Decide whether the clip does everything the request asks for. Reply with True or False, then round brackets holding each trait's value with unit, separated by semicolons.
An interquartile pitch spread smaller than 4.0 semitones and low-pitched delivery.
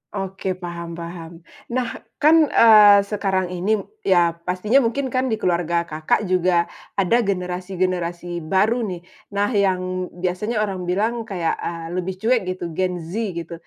False (3.2 semitones; 185 Hz)